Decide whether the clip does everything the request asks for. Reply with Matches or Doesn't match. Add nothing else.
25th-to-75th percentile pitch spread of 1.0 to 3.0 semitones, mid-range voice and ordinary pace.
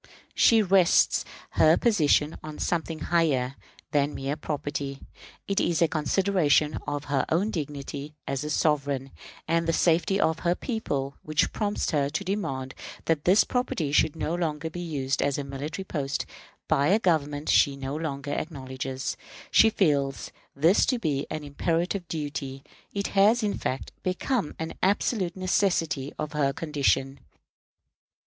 Doesn't match